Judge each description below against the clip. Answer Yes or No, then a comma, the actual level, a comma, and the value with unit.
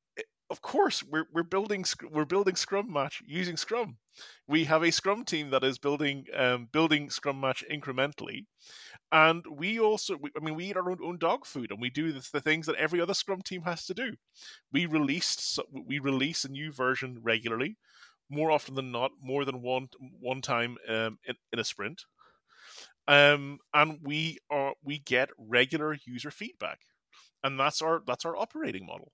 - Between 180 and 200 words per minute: Yes, average, 185 wpm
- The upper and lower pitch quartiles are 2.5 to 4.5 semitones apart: Yes, average, 4.0 semitones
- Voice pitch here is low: No, medium, 150 Hz